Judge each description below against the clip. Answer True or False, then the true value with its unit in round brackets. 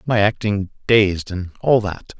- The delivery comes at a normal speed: True (165 wpm)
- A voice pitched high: False (100 Hz)